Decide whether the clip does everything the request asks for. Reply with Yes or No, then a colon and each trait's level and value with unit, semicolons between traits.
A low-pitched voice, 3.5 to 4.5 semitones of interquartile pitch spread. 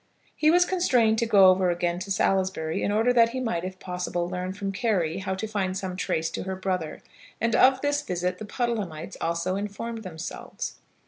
No: high, 190 Hz; average, 4.0 semitones